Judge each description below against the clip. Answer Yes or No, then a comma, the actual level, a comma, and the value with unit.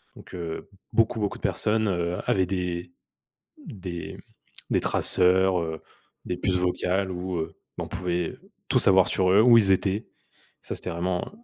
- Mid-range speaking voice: No, very low, 90 Hz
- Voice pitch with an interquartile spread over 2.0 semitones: No, narrow, 1.6 semitones